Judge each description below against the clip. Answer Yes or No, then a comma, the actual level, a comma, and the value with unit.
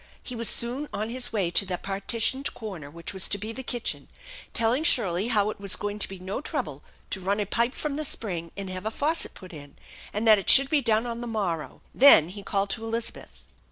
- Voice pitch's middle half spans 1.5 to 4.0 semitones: Yes, average, 3.6 semitones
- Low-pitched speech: No, high, 215 Hz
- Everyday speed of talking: No, fast, 230 wpm